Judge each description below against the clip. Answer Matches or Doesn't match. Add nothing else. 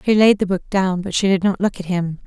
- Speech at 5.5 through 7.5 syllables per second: Matches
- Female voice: Matches